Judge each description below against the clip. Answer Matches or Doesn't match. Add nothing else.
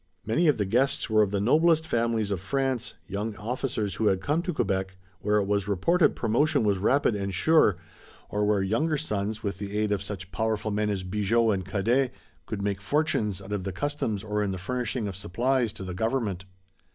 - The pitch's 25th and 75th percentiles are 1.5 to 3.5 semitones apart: Doesn't match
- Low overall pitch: Matches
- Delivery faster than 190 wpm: Matches